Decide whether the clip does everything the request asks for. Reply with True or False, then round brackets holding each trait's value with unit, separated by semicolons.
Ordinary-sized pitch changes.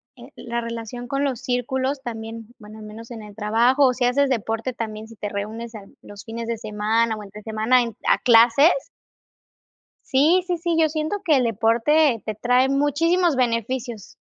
True (3.2 semitones)